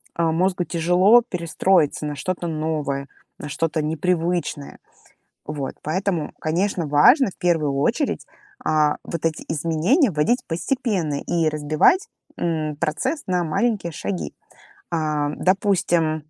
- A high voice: No, medium, 165 Hz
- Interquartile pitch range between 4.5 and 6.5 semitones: No, average, 3.2 semitones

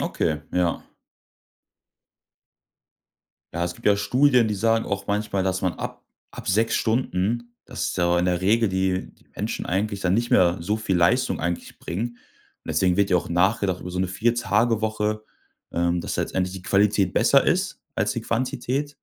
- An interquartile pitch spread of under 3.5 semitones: No, average, 3.8 semitones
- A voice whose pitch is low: Yes, low, 100 Hz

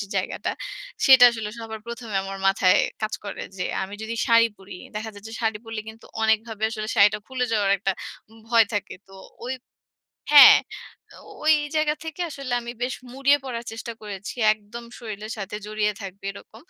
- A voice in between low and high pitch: No, high, 220 Hz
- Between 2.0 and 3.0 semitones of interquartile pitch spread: Yes, narrow, 2.4 semitones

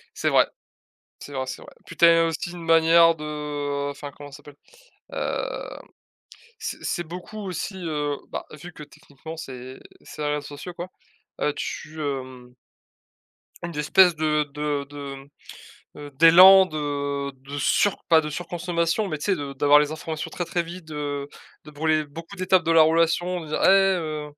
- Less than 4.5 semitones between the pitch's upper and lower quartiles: Yes, average, 2.8 semitones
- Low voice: No, medium, 155 Hz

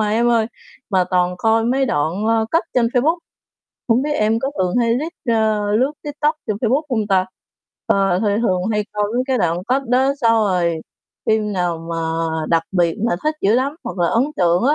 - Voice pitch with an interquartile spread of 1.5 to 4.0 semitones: No, average, 5.2 semitones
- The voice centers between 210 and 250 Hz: Yes, high, 220 Hz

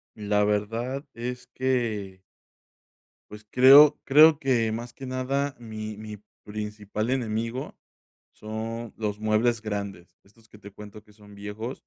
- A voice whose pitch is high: No, low, 110 Hz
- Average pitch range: Yes, average, 3.0 semitones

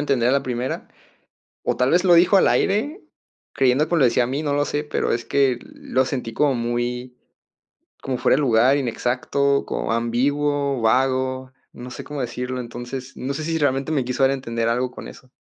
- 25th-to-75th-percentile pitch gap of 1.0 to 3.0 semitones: Yes, narrow, 2.6 semitones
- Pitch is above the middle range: No, low, 130 Hz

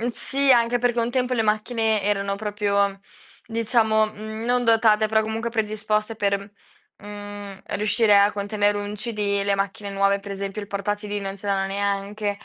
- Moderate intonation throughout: No, narrow, 1.8 semitones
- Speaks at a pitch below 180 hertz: No, high, 210 Hz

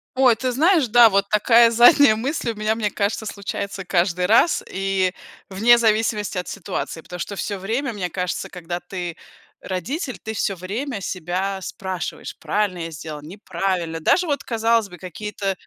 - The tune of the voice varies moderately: Yes, average, 3.9 semitones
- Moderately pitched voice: No, high, 200 Hz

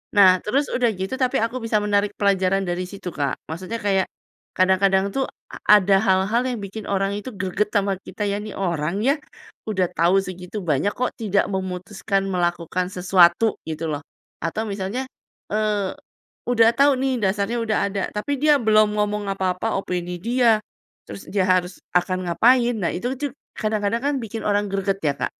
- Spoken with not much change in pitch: No, average, 3.1 semitones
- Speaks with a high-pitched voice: Yes, high, 200 Hz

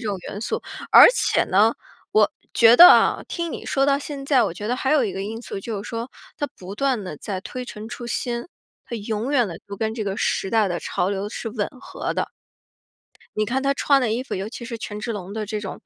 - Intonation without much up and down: No, average, 3.7 semitones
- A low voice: No, high, 225 Hz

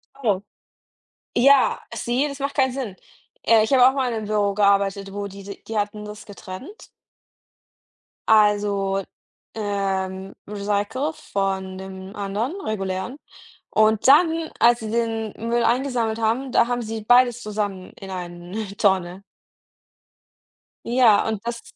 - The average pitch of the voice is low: No, high, 215 Hz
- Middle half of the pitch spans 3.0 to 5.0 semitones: Yes, average, 3.4 semitones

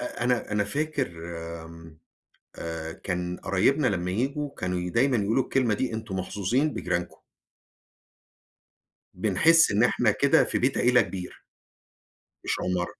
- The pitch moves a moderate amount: No, wide, 6.0 semitones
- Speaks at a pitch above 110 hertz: No, low, 105 Hz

